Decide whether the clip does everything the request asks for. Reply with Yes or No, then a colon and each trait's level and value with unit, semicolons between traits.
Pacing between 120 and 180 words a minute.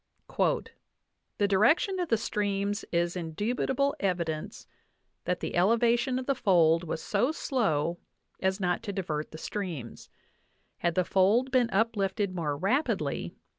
Yes: slow, 135 wpm